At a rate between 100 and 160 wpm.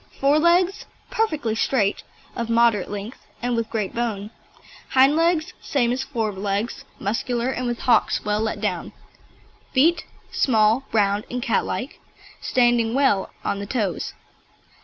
Yes: average, 140 wpm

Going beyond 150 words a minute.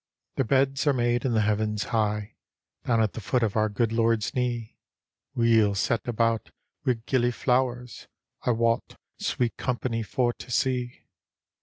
Yes: average, 160 wpm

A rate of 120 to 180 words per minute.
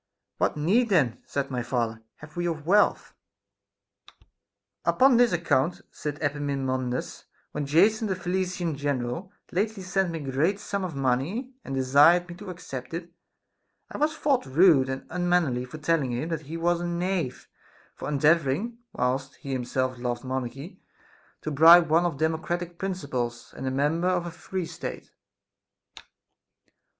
Yes: average, 150 wpm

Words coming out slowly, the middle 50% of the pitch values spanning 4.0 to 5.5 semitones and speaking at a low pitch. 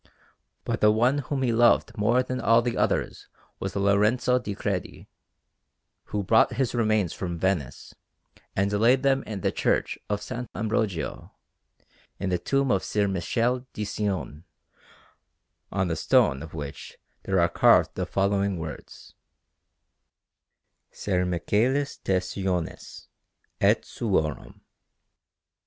Yes: slow, 130 wpm; average, 4.5 semitones; low, 100 Hz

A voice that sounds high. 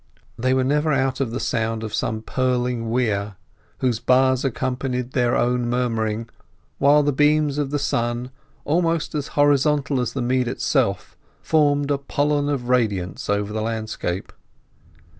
No: low, 125 Hz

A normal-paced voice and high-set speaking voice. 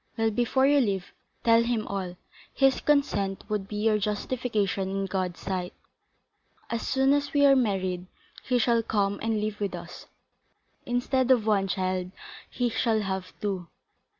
Yes: average, 155 wpm; high, 210 Hz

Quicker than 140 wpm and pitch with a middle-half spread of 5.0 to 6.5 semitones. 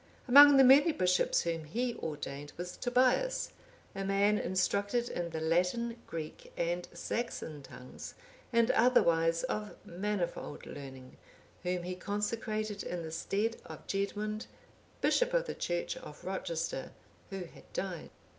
No: slow, 135 wpm; wide, 5.6 semitones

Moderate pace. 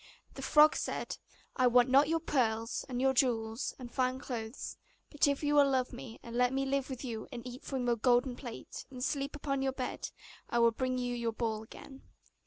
No: fast, 210 wpm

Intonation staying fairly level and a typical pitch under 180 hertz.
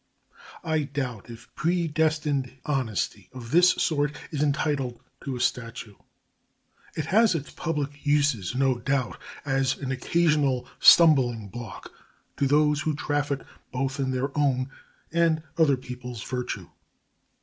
No: average, 3.1 semitones; medium, 140 Hz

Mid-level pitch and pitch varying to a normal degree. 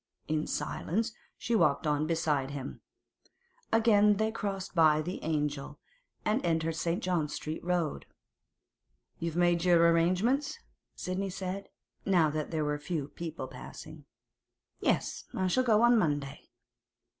Yes: medium, 170 Hz; average, 4.3 semitones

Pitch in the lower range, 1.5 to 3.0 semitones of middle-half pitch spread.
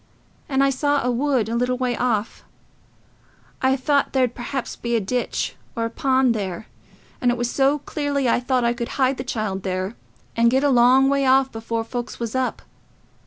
No: very high, 250 Hz; narrow, 2.4 semitones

